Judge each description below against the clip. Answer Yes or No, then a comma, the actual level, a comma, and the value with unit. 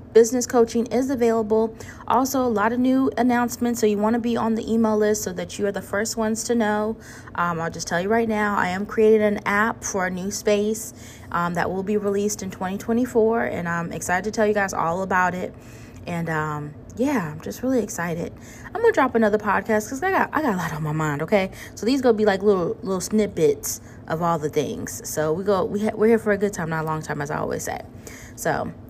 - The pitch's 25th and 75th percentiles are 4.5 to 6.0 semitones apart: Yes, average, 4.9 semitones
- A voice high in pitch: Yes, high, 210 Hz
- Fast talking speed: Yes, fast, 245 wpm